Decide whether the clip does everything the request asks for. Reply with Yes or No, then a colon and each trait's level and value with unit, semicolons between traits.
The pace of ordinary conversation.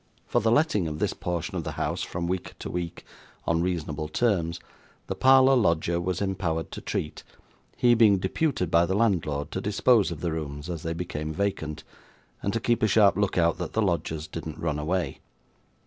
Yes: average, 195 wpm